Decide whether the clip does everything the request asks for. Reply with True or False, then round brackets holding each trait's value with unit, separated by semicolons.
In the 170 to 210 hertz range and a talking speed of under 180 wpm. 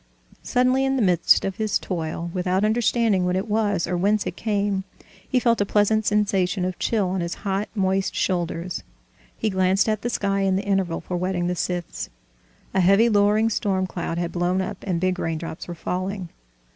False (190 Hz; 190 wpm)